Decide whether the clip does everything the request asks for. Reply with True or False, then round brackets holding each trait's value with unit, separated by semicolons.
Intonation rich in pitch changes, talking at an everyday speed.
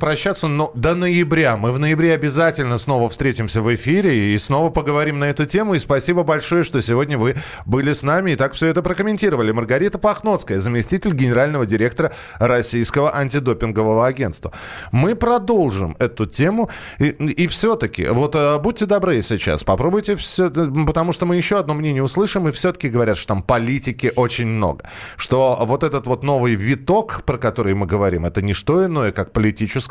False (6.2 semitones; 170 wpm)